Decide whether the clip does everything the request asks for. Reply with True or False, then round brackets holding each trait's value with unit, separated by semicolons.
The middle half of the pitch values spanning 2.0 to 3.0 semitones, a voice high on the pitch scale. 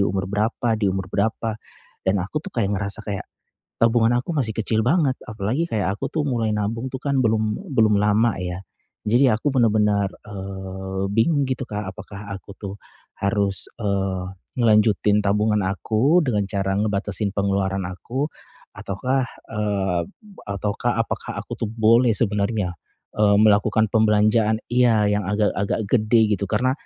False (2.6 semitones; 105 Hz)